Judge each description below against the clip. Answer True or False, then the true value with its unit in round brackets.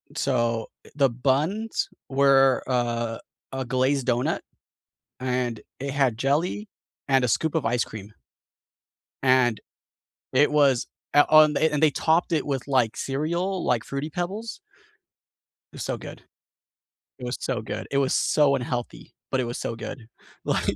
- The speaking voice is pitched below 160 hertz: True (135 Hz)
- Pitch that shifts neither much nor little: True (3.5 semitones)